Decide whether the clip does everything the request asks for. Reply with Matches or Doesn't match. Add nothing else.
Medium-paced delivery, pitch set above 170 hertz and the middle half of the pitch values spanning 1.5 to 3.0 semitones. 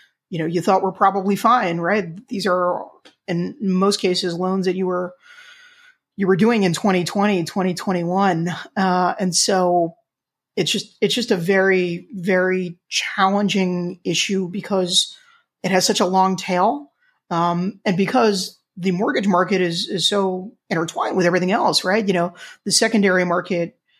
Matches